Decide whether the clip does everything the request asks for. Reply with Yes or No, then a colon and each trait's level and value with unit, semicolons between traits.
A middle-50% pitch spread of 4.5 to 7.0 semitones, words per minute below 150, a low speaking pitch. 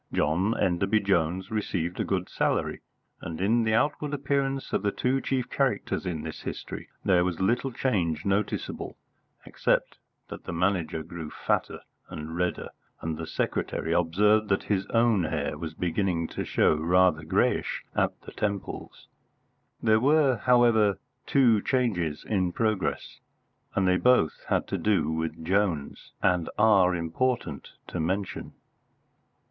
Yes: average, 4.9 semitones; average, 140 wpm; very low, 95 Hz